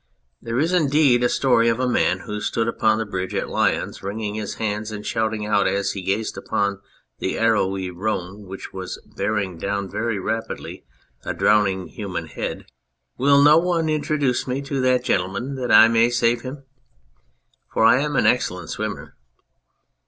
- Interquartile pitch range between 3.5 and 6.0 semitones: Yes, average, 4.2 semitones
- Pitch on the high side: No, low, 110 Hz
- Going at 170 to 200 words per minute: Yes, average, 175 wpm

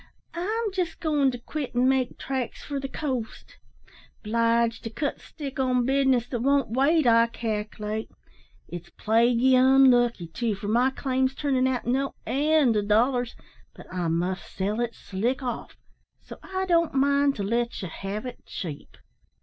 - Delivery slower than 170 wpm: Yes, average, 160 wpm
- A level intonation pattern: No, average, 3.4 semitones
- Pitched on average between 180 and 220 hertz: No, very high, 250 Hz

